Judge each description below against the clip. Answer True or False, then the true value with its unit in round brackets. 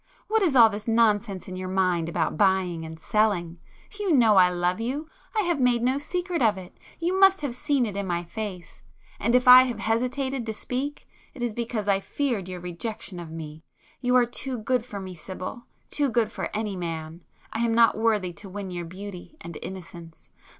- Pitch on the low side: False (215 Hz)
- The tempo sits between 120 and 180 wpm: False (190 wpm)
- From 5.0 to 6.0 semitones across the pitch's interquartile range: True (5.5 semitones)